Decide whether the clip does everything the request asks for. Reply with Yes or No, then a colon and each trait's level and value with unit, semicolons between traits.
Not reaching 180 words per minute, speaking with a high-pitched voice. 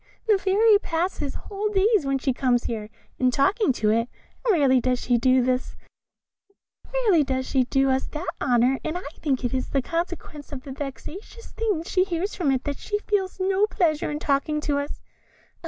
Yes: average, 170 wpm; very high, 295 Hz